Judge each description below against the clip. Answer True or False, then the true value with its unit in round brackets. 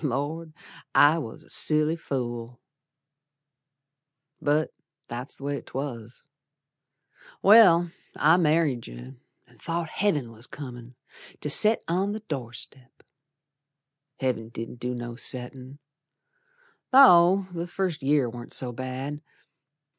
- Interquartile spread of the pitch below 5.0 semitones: False (5.3 semitones)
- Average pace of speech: False (115 wpm)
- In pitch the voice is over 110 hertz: True (140 Hz)